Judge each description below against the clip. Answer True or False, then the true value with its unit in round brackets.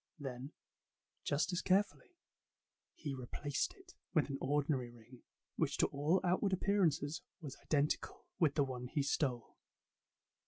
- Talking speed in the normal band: False (130 wpm)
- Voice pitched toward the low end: False (145 Hz)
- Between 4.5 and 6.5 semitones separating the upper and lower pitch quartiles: True (4.8 semitones)